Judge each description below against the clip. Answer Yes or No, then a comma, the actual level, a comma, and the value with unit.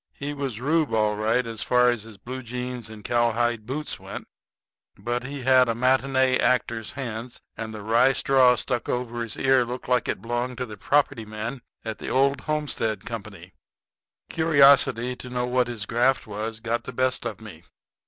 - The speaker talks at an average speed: Yes, average, 185 wpm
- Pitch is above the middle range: No, low, 125 Hz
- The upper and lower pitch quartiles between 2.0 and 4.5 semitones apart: Yes, narrow, 2.5 semitones